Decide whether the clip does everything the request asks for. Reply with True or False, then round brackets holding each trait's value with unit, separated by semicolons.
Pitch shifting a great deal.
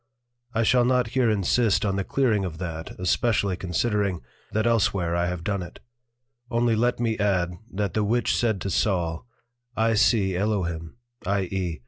False (4.1 semitones)